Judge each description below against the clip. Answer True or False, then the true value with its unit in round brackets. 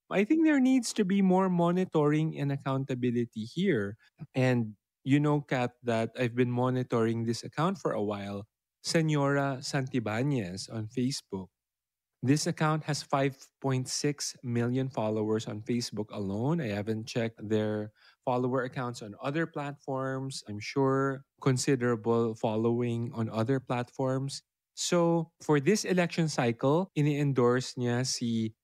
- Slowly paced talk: True (130 wpm)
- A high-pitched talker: False (130 Hz)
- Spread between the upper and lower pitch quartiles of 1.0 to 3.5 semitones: False (4.3 semitones)